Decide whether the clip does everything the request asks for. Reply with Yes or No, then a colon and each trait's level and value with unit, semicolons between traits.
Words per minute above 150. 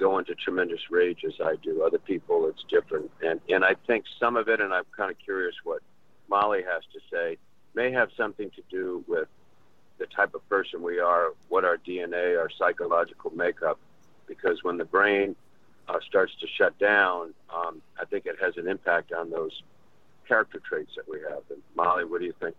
Yes: average, 200 wpm